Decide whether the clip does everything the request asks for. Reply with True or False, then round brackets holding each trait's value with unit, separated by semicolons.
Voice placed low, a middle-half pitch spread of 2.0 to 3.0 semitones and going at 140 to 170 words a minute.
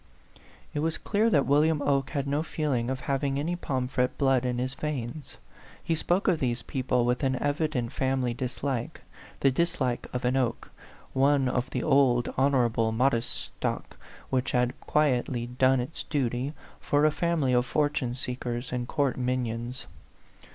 True (130 Hz; 2.7 semitones; 160 wpm)